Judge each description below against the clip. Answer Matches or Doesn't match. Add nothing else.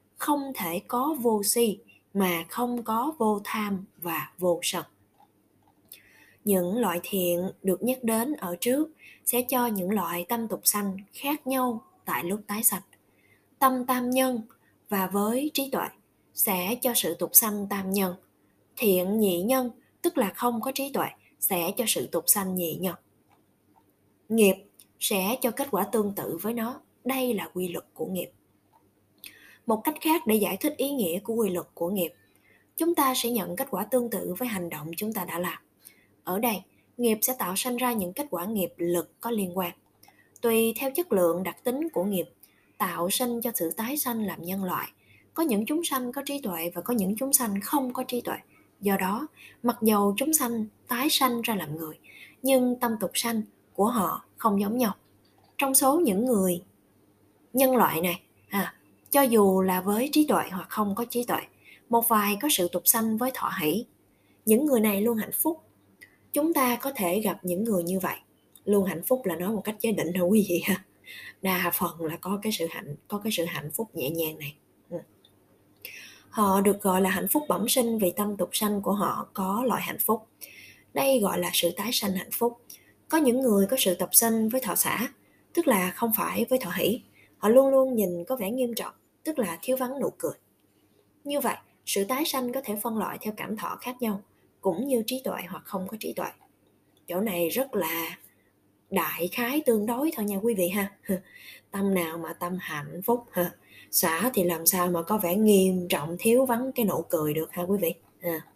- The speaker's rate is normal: Matches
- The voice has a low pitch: Doesn't match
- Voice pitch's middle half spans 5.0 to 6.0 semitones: Matches